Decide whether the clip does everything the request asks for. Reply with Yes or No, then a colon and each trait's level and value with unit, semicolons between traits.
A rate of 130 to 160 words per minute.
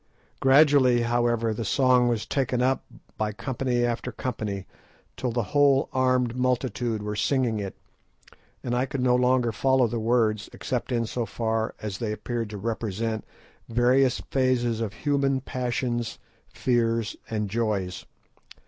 Yes: average, 145 wpm